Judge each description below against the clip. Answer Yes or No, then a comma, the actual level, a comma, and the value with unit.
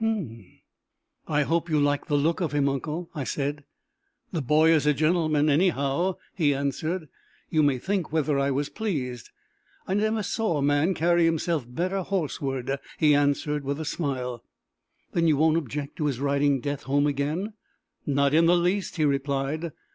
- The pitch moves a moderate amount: Yes, average, 3.1 semitones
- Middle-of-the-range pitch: Yes, medium, 150 Hz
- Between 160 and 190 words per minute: Yes, average, 170 wpm